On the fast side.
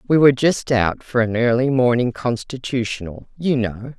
No: average, 165 wpm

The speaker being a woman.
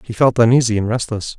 No: male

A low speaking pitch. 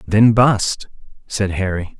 Yes: low, 100 Hz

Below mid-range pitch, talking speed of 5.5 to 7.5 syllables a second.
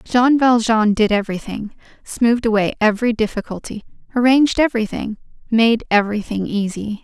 No: high, 225 Hz; 5.7 syllables/s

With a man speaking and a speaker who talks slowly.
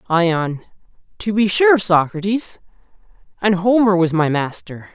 Yes: male; slow, 120 wpm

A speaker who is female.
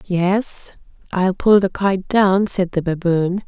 Yes: female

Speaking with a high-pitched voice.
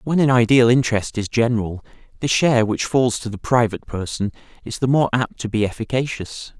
No: low, 120 Hz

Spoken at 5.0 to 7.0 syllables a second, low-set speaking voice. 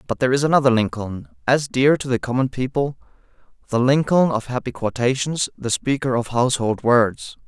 Yes: 5.4 syllables/s; low, 130 Hz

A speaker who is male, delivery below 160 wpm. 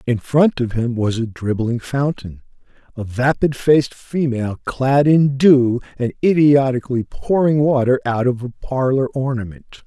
Yes: male; average, 145 wpm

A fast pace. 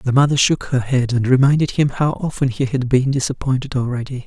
Yes: fast, 210 wpm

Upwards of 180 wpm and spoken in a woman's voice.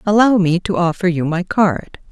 Yes: average, 200 wpm; female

